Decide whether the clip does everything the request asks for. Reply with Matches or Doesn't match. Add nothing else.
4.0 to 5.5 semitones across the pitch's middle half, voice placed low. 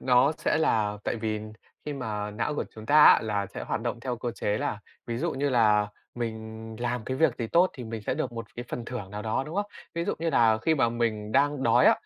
Doesn't match